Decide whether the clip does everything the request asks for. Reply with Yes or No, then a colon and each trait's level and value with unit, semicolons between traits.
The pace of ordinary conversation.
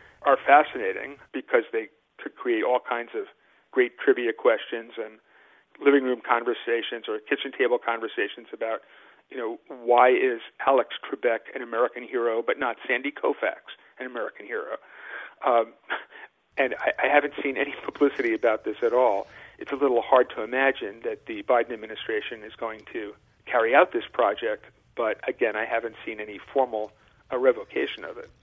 Yes: average, 165 wpm